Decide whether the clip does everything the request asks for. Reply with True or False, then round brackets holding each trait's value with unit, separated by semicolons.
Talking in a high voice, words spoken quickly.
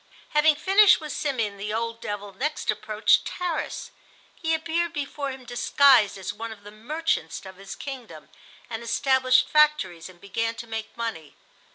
False (235 Hz; 160 wpm)